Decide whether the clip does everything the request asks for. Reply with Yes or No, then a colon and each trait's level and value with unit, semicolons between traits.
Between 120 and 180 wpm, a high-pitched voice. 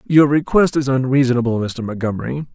No: average, 140 wpm; low, 130 Hz